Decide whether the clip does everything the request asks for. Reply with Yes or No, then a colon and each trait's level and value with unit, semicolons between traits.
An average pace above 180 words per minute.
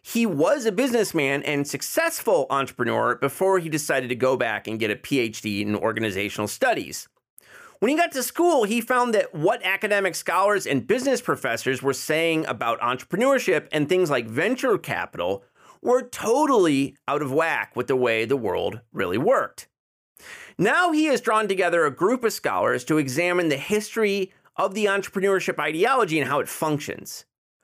No: average, 165 wpm